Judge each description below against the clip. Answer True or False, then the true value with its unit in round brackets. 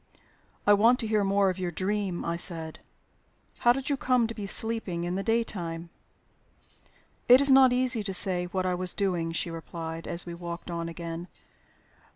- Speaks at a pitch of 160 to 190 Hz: True (185 Hz)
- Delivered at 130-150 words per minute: False (185 wpm)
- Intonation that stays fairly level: False (4.7 semitones)